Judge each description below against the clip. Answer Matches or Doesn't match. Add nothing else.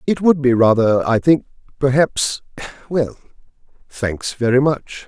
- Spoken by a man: Matches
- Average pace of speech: Doesn't match